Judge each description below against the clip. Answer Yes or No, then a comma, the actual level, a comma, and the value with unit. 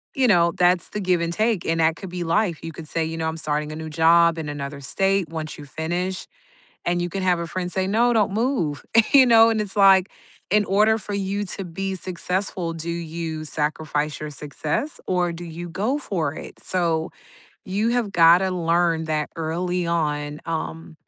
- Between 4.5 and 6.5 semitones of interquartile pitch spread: No, average, 3.2 semitones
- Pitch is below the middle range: No, medium, 170 Hz